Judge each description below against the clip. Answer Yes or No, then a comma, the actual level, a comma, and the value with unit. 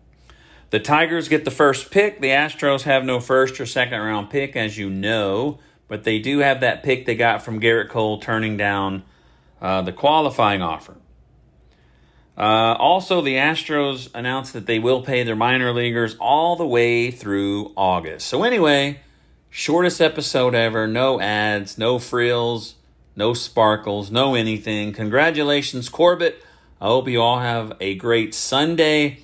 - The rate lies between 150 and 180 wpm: Yes, average, 155 wpm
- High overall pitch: No, low, 120 Hz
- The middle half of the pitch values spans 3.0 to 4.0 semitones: No, average, 4.7 semitones